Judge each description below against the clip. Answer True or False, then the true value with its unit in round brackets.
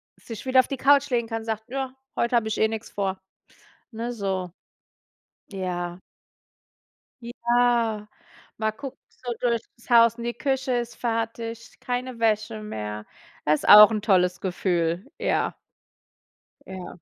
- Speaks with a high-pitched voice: True (225 Hz)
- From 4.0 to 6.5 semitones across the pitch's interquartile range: False (3.6 semitones)